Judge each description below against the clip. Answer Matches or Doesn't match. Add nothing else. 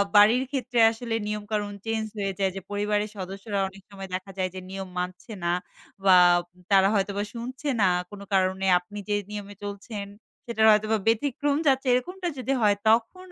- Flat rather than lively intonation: Doesn't match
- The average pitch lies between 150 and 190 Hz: Doesn't match